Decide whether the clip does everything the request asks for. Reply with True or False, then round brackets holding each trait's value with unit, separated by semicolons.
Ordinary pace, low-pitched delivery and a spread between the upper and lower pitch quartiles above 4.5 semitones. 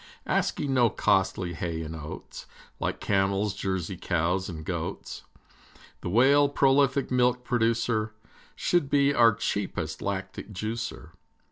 False (120 wpm; 110 Hz; 5.0 semitones)